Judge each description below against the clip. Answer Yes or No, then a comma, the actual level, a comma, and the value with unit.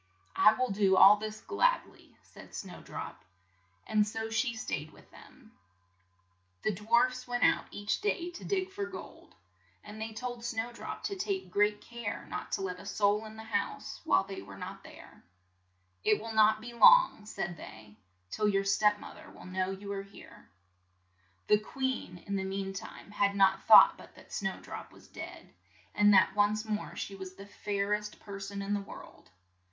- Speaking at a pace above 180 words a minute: Yes, average, 190 wpm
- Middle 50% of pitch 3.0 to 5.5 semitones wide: No, narrow, 2.4 semitones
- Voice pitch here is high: Yes, high, 210 Hz